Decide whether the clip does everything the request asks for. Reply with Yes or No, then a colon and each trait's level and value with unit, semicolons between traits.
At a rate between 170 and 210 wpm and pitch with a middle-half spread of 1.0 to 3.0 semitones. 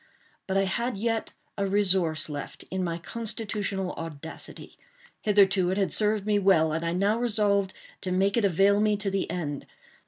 Yes: average, 175 wpm; narrow, 2.6 semitones